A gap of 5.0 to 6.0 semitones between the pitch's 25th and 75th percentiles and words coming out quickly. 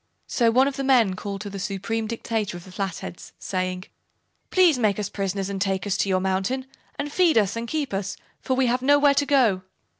Yes: average, 5.3 semitones; fast, 210 wpm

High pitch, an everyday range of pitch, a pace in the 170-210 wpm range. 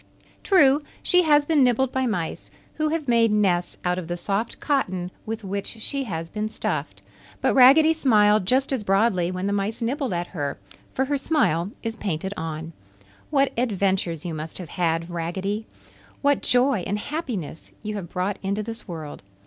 No: high, 210 Hz; wide, 6.6 semitones; average, 175 wpm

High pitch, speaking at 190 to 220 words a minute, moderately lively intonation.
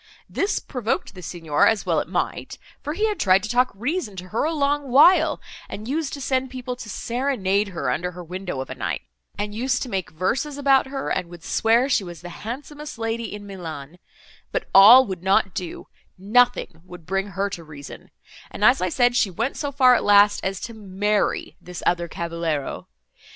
No: high, 210 Hz; average, 195 wpm; wide, 6.3 semitones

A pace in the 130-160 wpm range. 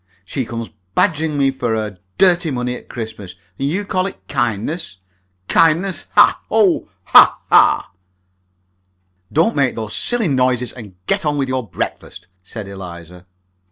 Yes: average, 145 wpm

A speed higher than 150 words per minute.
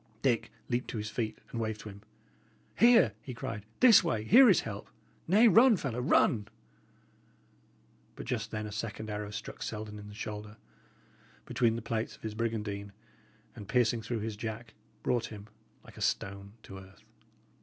Yes: average, 170 wpm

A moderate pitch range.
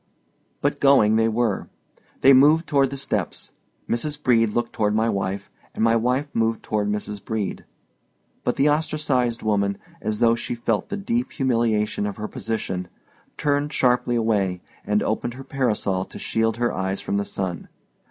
Yes: average, 4.0 semitones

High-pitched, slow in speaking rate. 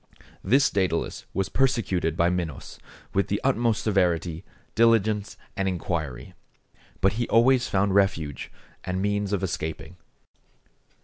No: very low, 95 Hz; slow, 120 wpm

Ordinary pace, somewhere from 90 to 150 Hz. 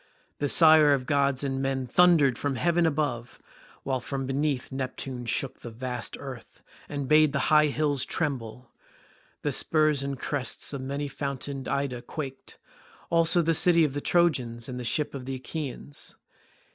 Yes: average, 165 wpm; medium, 140 Hz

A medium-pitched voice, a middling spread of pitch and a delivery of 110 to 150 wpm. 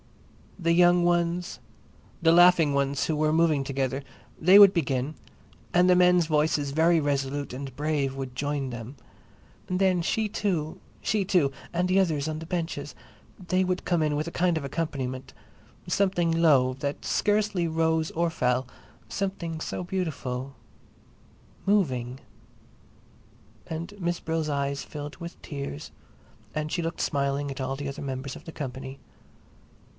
Yes: medium, 155 Hz; average, 4.0 semitones; average, 145 wpm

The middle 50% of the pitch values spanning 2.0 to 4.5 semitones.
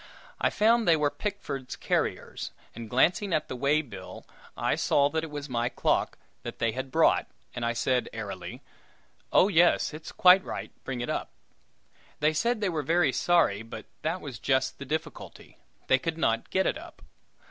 No: wide, 5.5 semitones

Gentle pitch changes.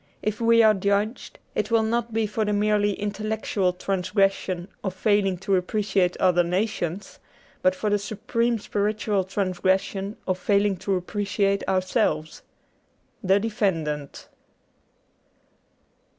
Yes: narrow, 2.3 semitones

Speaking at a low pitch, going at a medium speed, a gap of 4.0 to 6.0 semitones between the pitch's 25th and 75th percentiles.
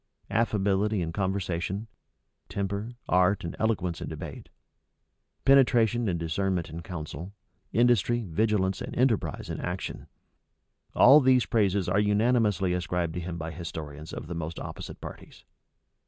No: very low, 95 Hz; slow, 130 wpm; average, 4.3 semitones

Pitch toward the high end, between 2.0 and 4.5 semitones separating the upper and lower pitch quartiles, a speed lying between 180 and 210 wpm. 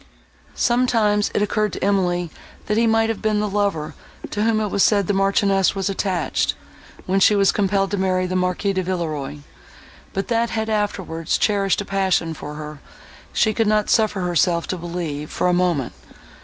Yes: high, 195 Hz; average, 2.9 semitones; average, 185 wpm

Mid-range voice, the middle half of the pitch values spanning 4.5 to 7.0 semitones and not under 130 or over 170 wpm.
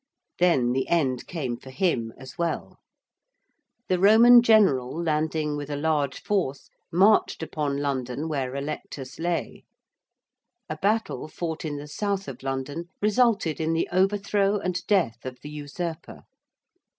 Yes: medium, 160 Hz; average, 5.2 semitones; average, 140 wpm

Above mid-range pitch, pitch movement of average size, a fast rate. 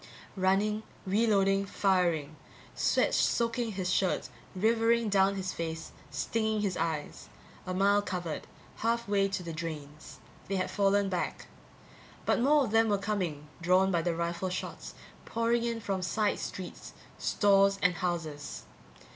No: high, 195 Hz; average, 3.2 semitones; average, 145 wpm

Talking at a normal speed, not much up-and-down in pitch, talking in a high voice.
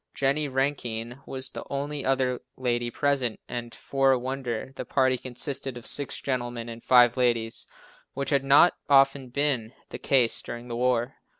No: average, 165 wpm; narrow, 2.2 semitones; low, 130 Hz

